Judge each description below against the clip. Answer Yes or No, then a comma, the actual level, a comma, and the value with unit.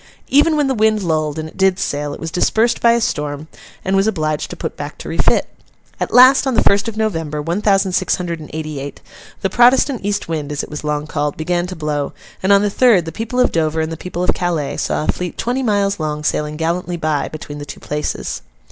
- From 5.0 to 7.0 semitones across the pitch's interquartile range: Yes, wide, 5.4 semitones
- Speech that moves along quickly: Yes, fast, 240 wpm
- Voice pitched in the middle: Yes, medium, 170 Hz